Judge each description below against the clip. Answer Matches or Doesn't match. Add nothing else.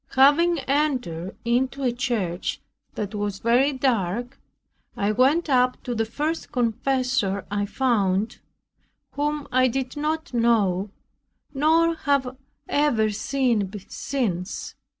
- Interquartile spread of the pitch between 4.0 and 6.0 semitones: Matches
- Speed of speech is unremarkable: Doesn't match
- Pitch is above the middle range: Matches